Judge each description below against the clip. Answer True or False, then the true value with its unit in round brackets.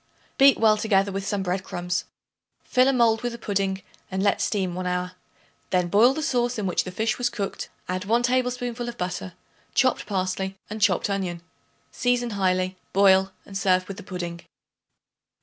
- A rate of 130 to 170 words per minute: False (180 wpm)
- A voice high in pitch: True (195 Hz)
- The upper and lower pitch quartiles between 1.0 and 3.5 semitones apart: False (4.3 semitones)